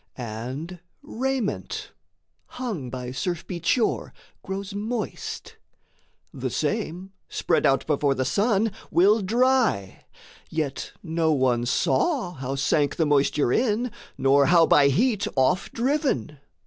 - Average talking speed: No, slow, 120 wpm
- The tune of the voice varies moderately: No, wide, 8.1 semitones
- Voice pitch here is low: No, medium, 170 Hz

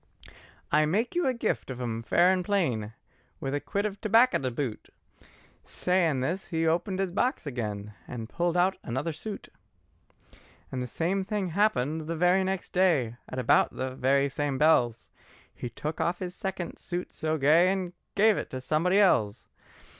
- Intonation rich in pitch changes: Yes, wide, 6.5 semitones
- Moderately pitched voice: Yes, medium, 165 Hz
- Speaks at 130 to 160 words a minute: No, average, 175 wpm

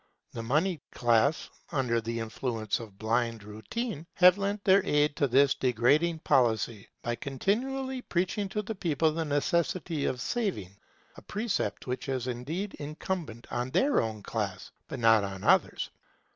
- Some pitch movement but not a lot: No, wide, 8.0 semitones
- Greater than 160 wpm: No, average, 150 wpm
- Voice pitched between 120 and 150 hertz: Yes, medium, 140 Hz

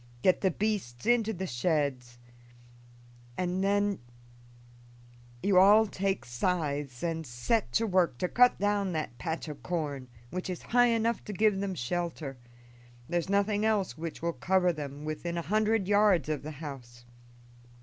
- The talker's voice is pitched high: No, medium, 180 Hz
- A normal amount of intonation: No, wide, 5.7 semitones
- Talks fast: No, average, 155 wpm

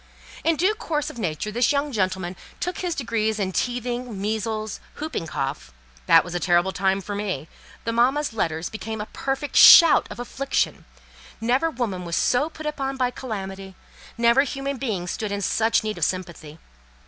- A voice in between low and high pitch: No, high, 225 Hz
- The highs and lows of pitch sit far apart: Yes, wide, 6.0 semitones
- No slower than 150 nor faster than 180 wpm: Yes, average, 170 wpm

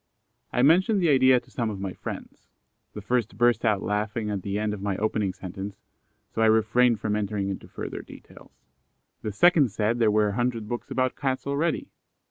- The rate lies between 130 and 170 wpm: No, average, 195 wpm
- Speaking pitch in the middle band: No, low, 110 Hz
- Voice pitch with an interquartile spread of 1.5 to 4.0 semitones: Yes, average, 3.3 semitones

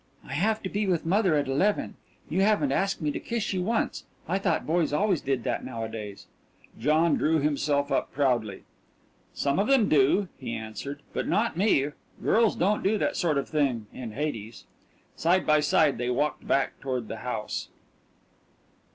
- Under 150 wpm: No, average, 175 wpm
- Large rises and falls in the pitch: Yes, wide, 6.5 semitones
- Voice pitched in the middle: Yes, medium, 150 Hz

